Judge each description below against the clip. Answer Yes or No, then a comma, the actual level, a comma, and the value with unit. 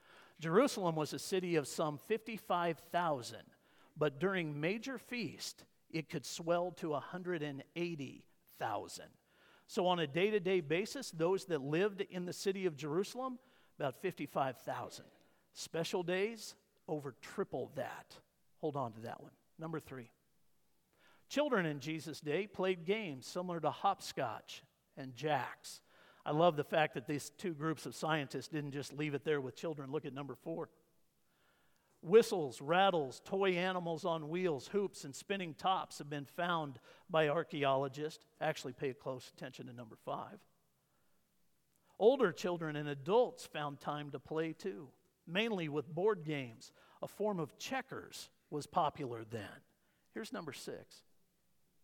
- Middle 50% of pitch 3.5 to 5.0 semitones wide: Yes, average, 4.2 semitones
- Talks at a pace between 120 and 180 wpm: Yes, average, 140 wpm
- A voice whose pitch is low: No, medium, 160 Hz